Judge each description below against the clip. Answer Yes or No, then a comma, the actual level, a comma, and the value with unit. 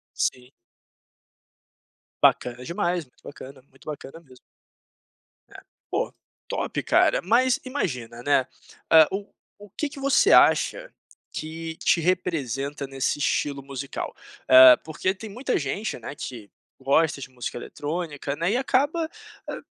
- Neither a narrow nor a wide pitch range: No, wide, 6.3 semitones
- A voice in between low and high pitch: Yes, medium, 155 Hz